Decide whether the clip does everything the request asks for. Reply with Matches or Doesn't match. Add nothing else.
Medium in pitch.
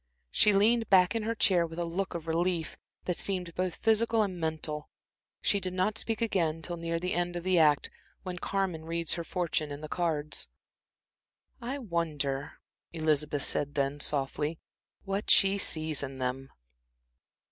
Matches